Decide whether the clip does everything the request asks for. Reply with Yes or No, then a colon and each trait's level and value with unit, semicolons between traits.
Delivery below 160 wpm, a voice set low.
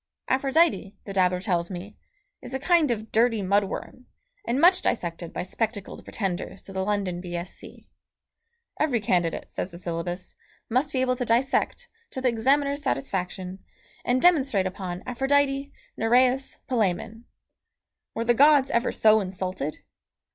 No: average, 140 wpm; high, 225 Hz